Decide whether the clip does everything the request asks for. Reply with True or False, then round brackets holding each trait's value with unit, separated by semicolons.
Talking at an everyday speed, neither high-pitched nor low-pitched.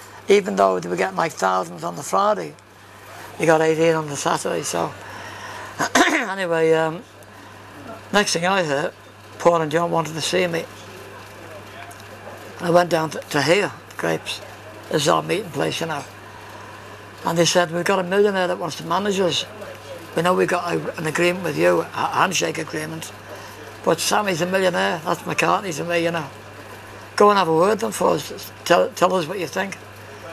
True (190 wpm; 160 Hz)